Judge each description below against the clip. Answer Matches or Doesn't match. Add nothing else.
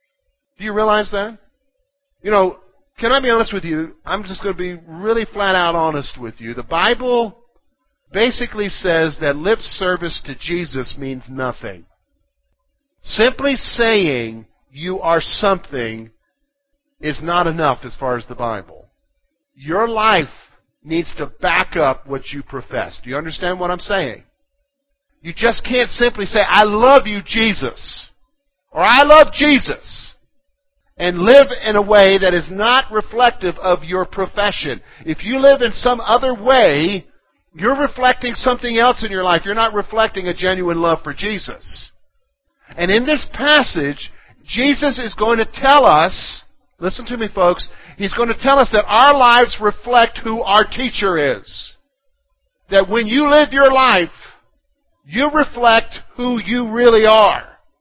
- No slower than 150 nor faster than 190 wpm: Matches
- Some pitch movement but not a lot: Doesn't match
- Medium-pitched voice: Doesn't match